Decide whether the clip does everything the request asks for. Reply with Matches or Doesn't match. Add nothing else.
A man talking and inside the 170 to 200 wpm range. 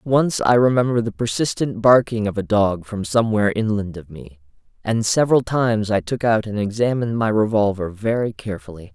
Matches